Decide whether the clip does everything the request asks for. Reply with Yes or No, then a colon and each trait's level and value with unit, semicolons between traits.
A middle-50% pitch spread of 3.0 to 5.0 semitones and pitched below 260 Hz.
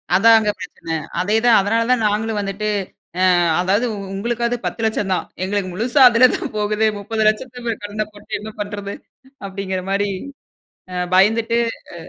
No: narrow, 2.5 semitones; high, 210 Hz